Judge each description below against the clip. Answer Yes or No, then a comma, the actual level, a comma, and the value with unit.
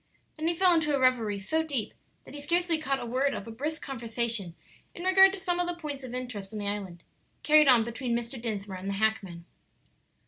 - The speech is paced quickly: Yes, fast, 220 wpm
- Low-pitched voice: No, very high, 255 Hz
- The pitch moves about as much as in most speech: No, wide, 6.3 semitones